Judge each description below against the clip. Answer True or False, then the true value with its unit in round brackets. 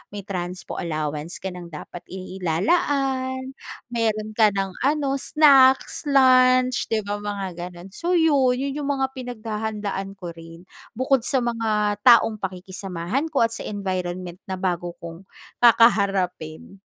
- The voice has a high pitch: True (210 Hz)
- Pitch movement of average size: False (6.0 semitones)